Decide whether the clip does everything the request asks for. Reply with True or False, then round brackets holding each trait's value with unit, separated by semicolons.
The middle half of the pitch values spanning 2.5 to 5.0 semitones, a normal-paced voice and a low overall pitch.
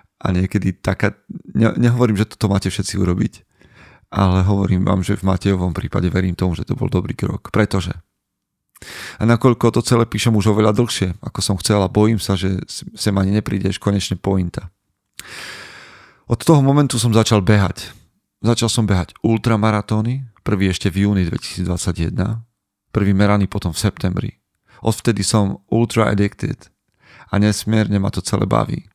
True (2.9 semitones; 155 wpm; 100 Hz)